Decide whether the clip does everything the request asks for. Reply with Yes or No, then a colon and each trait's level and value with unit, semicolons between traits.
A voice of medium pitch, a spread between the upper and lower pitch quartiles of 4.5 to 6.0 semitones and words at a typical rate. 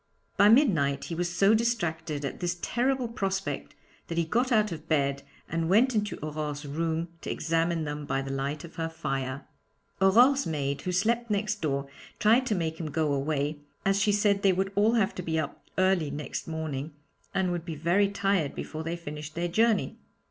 Yes: medium, 170 Hz; average, 5.0 semitones; average, 190 wpm